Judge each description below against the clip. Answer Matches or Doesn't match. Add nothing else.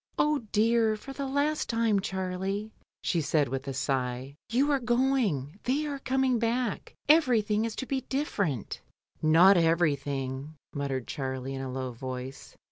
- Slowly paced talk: Doesn't match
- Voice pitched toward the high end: Matches